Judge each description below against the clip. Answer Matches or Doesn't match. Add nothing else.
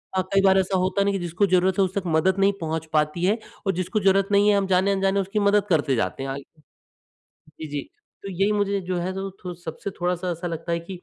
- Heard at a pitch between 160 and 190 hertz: Matches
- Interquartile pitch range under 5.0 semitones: Matches